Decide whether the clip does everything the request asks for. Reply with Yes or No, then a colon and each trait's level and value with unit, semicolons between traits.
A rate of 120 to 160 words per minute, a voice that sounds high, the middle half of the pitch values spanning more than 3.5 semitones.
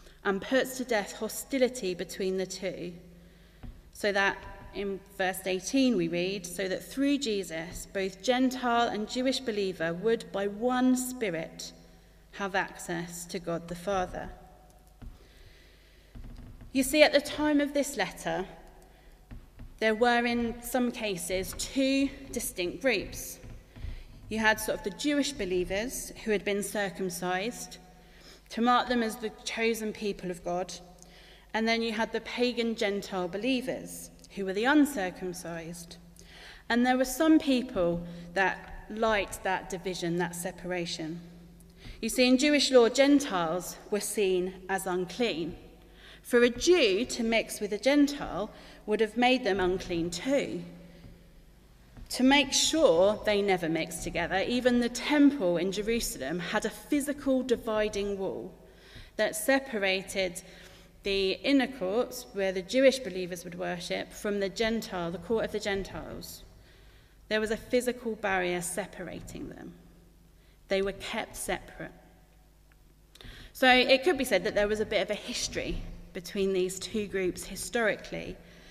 Yes: average, 140 wpm; high, 200 Hz; average, 5.1 semitones